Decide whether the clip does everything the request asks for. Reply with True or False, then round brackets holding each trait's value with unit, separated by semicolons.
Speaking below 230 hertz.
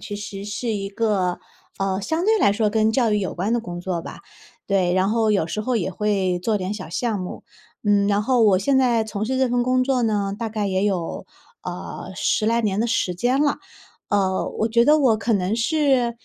True (210 Hz)